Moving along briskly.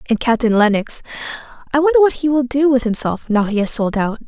Yes: fast, 210 wpm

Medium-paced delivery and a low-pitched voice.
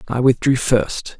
Yes: average, 150 wpm; low, 125 Hz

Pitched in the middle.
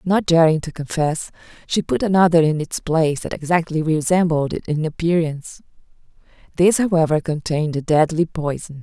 Yes: medium, 160 Hz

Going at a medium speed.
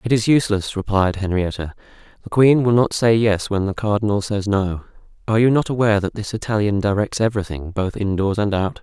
Yes: average, 195 wpm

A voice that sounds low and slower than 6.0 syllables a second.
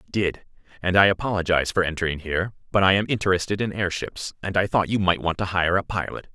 No: very low, 95 Hz; 6.4 syllables/s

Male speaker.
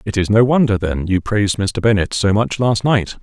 Yes: male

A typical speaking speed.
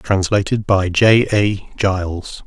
No: slow, 120 wpm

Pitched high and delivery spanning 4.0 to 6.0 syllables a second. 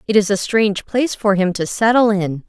Yes: high, 205 Hz; 5.6 syllables/s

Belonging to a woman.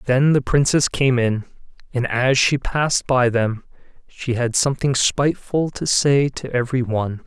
No: male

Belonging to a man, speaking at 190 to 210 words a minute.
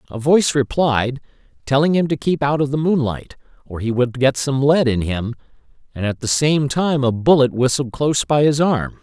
Yes: male; fast, 205 wpm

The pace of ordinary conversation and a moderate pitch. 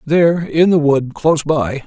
Yes: average, 195 wpm; medium, 150 Hz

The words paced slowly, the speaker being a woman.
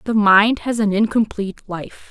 No: average, 170 wpm; female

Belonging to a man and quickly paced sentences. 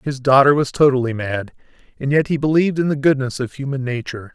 No: male; average, 195 wpm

